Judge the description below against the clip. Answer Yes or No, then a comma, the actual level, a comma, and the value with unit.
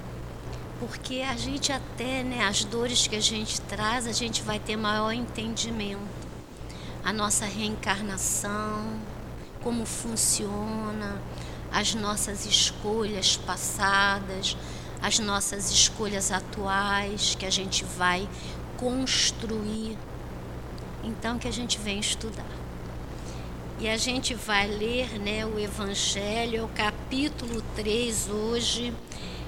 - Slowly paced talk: Yes, slow, 110 wpm